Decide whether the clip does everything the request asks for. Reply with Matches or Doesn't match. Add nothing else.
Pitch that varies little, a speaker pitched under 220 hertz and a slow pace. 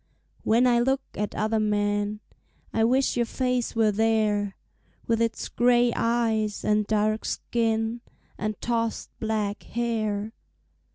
Doesn't match